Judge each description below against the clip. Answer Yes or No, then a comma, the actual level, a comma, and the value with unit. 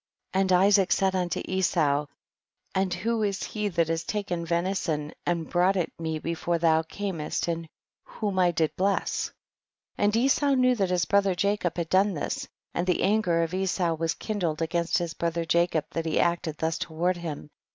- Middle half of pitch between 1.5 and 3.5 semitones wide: Yes, average, 2.8 semitones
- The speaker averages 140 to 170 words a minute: No, average, 185 wpm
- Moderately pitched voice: Yes, medium, 175 Hz